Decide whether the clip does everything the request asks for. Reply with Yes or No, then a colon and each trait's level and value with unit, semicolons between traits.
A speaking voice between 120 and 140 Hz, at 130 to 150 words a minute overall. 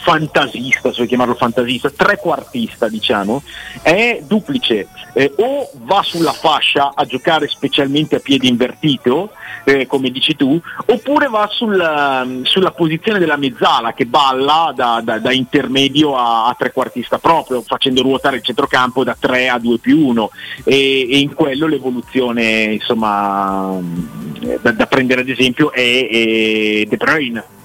Yes: low, 135 Hz; average, 140 wpm